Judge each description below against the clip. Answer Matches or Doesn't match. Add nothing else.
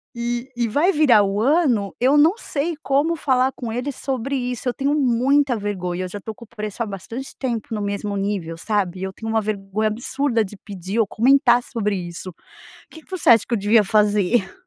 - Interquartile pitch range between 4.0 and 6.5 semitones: Matches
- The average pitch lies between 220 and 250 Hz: Matches